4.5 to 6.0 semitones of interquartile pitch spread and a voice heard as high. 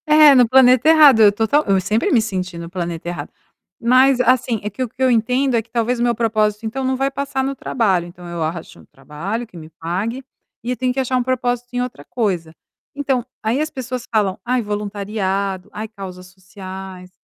Yes: average, 5.1 semitones; high, 225 Hz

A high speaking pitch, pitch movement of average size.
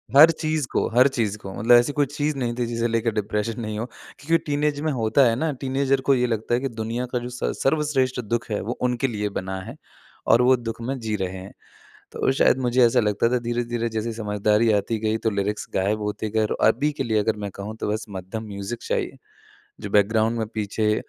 No: low, 115 Hz; average, 3.2 semitones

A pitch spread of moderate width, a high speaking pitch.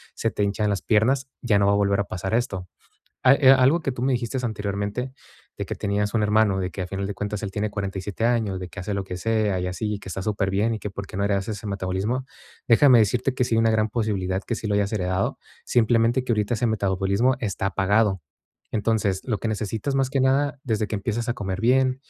No: average, 3.2 semitones; low, 105 Hz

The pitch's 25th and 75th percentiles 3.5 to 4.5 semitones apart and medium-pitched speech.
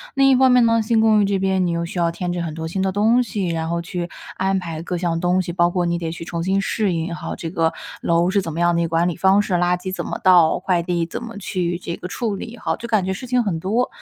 No: average, 3.0 semitones; medium, 180 Hz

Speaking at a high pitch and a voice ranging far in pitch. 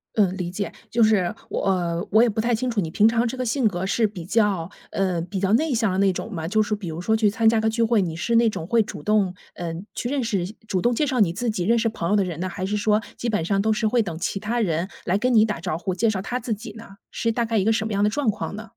No: high, 210 Hz; average, 3.5 semitones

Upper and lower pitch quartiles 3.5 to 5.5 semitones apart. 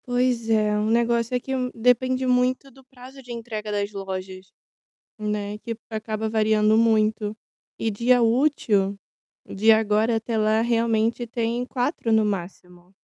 No: narrow, 2.6 semitones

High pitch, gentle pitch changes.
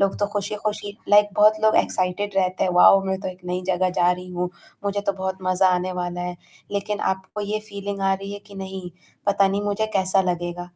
Yes: high, 195 Hz; narrow, 1.9 semitones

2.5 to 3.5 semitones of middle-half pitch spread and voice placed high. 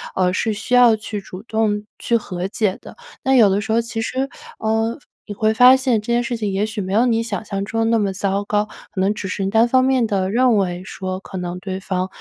Yes: average, 3.0 semitones; high, 215 Hz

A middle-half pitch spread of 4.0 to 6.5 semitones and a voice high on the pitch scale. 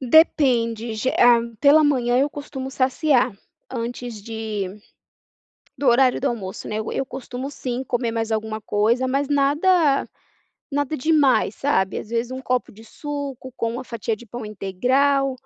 No: average, 3.3 semitones; very high, 250 Hz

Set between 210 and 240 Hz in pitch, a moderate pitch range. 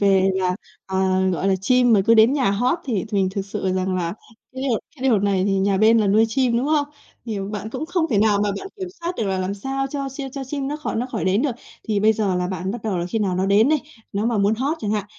Yes: high, 215 Hz; average, 5.0 semitones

